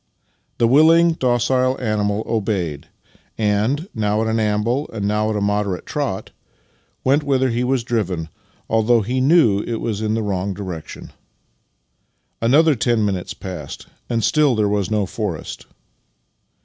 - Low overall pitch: Yes, low, 110 Hz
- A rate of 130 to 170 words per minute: Yes, average, 150 wpm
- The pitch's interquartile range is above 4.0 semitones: No, average, 3.5 semitones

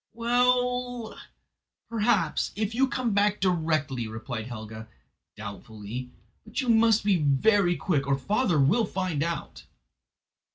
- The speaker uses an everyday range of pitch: No, wide, 9.0 semitones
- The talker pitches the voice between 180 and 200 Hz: Yes, medium, 185 Hz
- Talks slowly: Yes, slow, 120 wpm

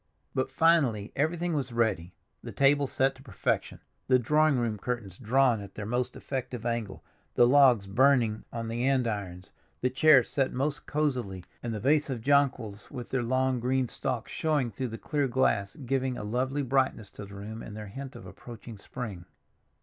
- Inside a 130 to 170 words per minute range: No, average, 180 wpm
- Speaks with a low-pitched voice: Yes, low, 125 Hz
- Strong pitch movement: No, average, 3.7 semitones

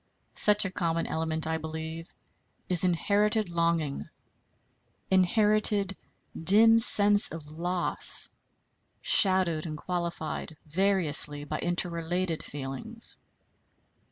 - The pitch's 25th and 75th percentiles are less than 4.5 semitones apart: Yes, average, 3.6 semitones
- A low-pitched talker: No, medium, 175 Hz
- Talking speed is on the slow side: Yes, slow, 90 wpm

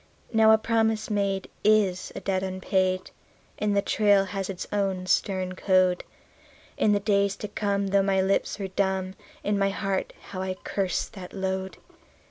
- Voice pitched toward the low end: No, high, 195 Hz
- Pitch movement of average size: No, narrow, 1.4 semitones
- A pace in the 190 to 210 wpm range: No, average, 165 wpm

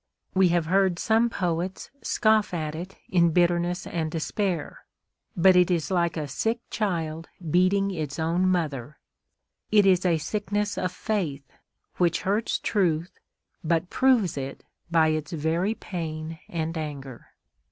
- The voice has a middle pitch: Yes, medium, 175 Hz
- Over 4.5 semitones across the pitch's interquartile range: No, average, 3.3 semitones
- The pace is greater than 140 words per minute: No, slow, 135 wpm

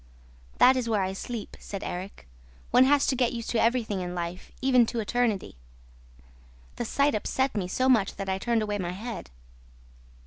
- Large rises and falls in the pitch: No, average, 4.4 semitones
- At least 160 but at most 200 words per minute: Yes, average, 180 wpm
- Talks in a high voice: Yes, high, 225 Hz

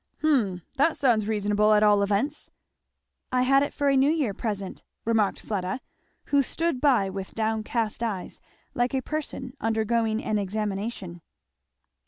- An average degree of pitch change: Yes, average, 4.4 semitones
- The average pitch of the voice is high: Yes, high, 220 Hz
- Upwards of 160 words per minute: No, average, 155 wpm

